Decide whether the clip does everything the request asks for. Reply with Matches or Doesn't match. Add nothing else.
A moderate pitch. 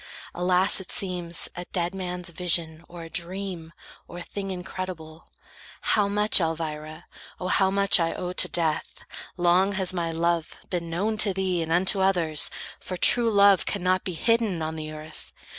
Matches